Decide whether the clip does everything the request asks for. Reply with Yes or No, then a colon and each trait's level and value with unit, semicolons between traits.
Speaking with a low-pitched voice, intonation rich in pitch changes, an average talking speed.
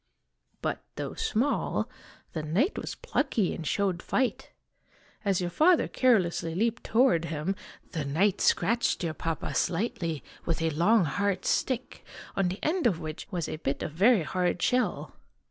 No: medium, 185 Hz; wide, 5.9 semitones; average, 160 wpm